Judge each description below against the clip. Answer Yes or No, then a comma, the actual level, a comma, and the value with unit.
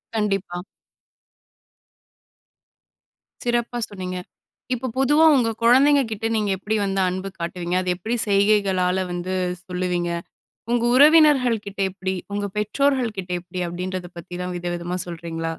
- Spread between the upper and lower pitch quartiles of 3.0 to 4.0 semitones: No, average, 4.4 semitones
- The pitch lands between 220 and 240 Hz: No, high, 195 Hz